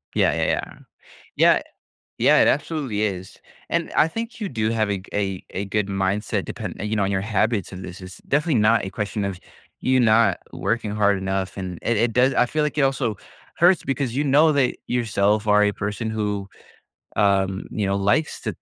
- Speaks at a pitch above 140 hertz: No, low, 105 Hz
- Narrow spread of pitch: No, average, 4.5 semitones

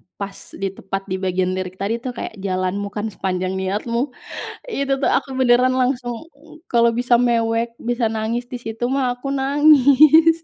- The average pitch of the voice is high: Yes, high, 235 Hz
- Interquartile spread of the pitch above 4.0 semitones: Yes, average, 4.6 semitones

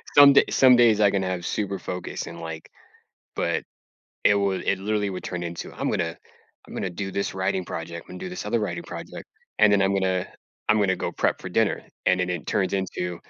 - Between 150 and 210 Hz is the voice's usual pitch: No, very low, 95 Hz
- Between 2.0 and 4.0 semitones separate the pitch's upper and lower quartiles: Yes, narrow, 2.4 semitones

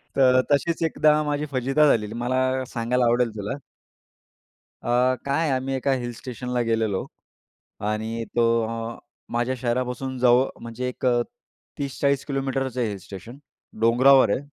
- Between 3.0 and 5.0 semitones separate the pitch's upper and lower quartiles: No, narrow, 2.5 semitones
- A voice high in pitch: No, low, 125 Hz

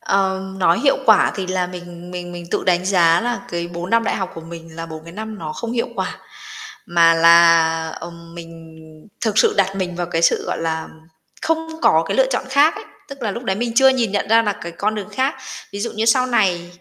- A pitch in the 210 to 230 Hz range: No, medium, 185 Hz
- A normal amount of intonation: Yes, average, 4.9 semitones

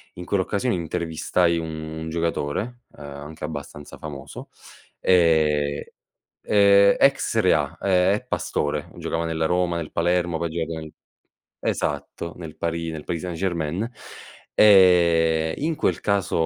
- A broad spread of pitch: No, narrow, 2.4 semitones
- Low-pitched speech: Yes, very low, 85 Hz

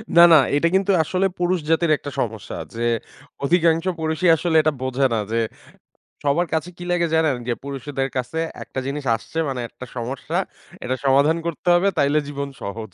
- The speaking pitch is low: No, medium, 145 Hz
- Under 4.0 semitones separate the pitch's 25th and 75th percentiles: No, average, 4.3 semitones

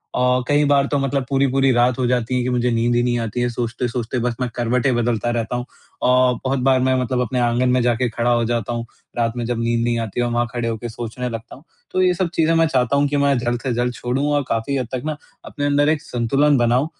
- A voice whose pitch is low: Yes, low, 125 Hz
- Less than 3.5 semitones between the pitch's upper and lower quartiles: Yes, narrow, 2.4 semitones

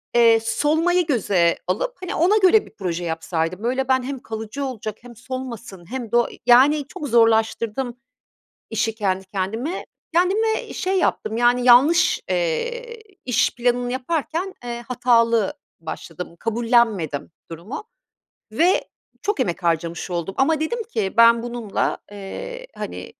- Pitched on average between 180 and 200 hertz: No, high, 240 Hz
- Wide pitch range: Yes, wide, 6.3 semitones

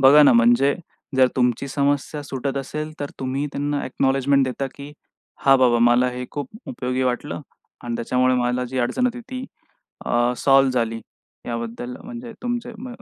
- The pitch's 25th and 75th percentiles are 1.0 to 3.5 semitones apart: Yes, narrow, 2.6 semitones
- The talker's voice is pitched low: Yes, low, 130 Hz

